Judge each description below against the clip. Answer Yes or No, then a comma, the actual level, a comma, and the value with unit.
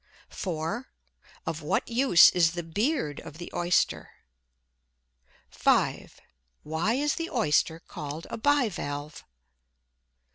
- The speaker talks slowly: Yes, slow, 110 wpm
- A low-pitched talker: No, medium, 175 Hz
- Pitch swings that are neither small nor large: No, wide, 7.2 semitones